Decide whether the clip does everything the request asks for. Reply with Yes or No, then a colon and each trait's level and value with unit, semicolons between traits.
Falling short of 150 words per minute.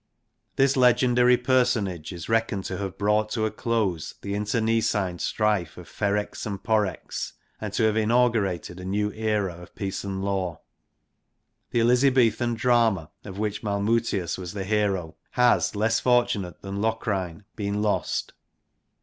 Yes: average, 140 wpm